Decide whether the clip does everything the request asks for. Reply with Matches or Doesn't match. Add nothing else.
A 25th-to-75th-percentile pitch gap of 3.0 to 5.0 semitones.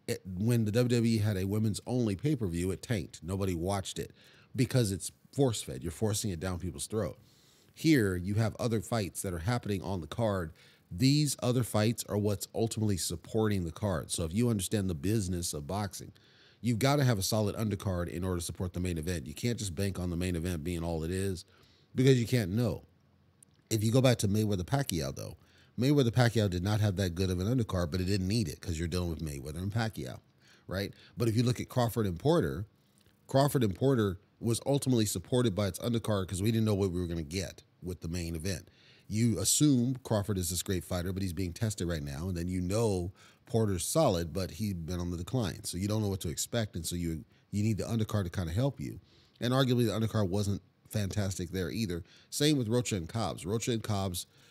Matches